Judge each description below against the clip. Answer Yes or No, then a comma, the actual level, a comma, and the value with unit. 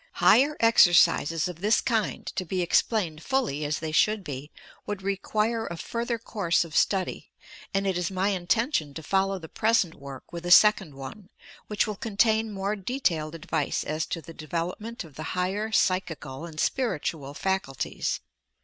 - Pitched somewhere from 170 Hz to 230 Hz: Yes, medium, 185 Hz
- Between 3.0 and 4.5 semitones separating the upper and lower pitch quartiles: No, average, 4.9 semitones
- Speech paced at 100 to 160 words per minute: No, average, 175 wpm